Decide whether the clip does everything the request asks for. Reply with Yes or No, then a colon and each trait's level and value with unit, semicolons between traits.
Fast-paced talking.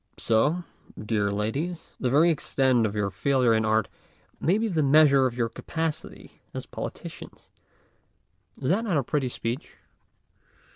No: average, 145 wpm